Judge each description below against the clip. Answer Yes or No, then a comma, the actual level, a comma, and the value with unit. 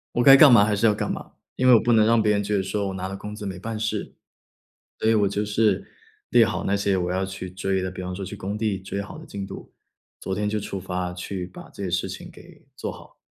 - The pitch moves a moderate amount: No, narrow, 2.2 semitones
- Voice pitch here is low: Yes, low, 100 Hz